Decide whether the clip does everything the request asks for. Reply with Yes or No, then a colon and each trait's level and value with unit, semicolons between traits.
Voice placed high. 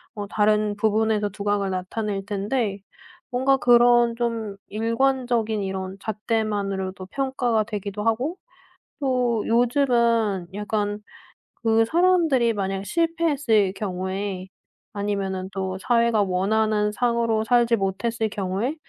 Yes: high, 220 Hz